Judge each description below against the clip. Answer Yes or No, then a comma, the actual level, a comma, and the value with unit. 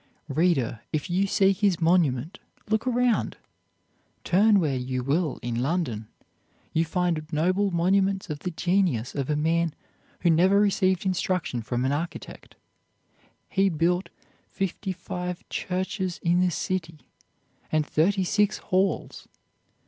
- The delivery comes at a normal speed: No, slow, 130 wpm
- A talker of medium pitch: Yes, medium, 175 Hz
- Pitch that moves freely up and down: No, average, 3.7 semitones